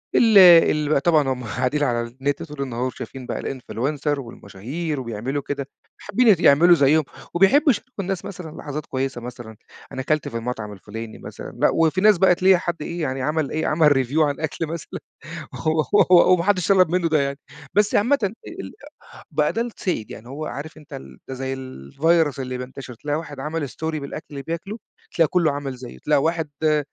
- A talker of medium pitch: Yes, medium, 150 Hz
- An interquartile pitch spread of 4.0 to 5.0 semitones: Yes, average, 4.3 semitones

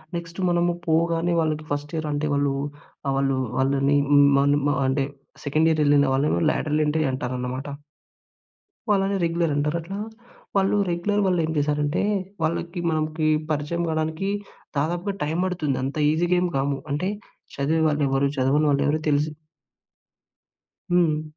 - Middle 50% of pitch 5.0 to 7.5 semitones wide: No, average, 3.0 semitones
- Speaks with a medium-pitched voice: Yes, medium, 155 Hz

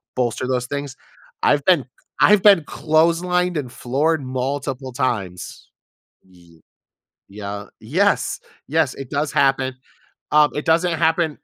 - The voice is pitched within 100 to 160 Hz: Yes, medium, 140 Hz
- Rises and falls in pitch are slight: No, average, 4.2 semitones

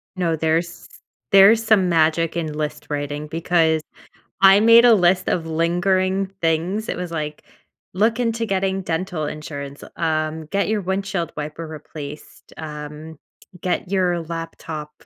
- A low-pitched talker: No, medium, 170 Hz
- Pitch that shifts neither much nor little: Yes, average, 3.6 semitones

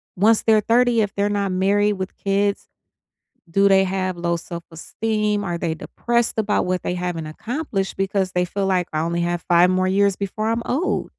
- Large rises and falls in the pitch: No, average, 2.7 semitones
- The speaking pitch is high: Yes, high, 195 Hz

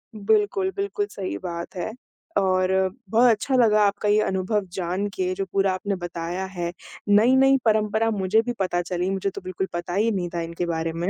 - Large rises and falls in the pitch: No, average, 3.3 semitones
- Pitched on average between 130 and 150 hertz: No, high, 195 Hz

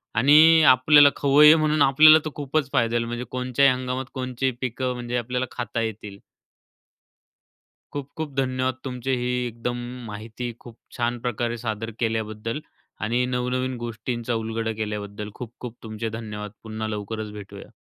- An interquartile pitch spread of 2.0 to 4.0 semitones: Yes, narrow, 2.6 semitones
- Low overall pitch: Yes, low, 120 Hz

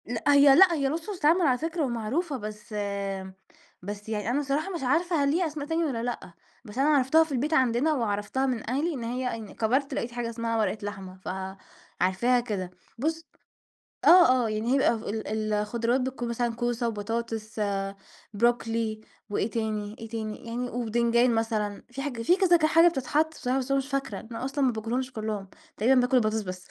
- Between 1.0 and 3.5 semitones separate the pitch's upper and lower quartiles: No, average, 4.1 semitones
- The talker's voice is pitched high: Yes, high, 240 Hz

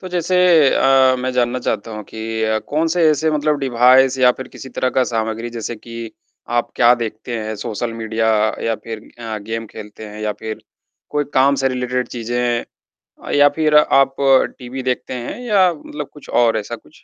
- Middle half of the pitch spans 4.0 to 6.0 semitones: No, average, 3.2 semitones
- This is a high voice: No, low, 125 Hz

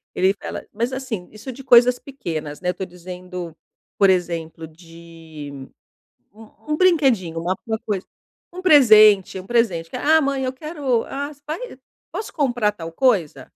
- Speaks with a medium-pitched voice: No, high, 210 Hz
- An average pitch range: No, wide, 7.2 semitones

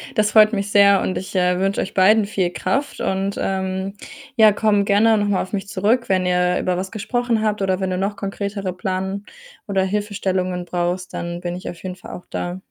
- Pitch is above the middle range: Yes, high, 195 Hz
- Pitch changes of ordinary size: No, narrow, 2.0 semitones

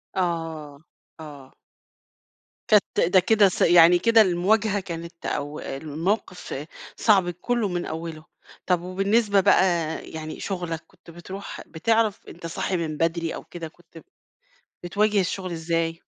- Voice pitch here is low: No, medium, 175 Hz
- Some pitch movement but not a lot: Yes, average, 3.2 semitones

